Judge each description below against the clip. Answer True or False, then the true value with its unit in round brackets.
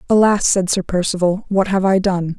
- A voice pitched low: False (190 Hz)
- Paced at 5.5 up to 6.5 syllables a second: True (5.6 syllables/s)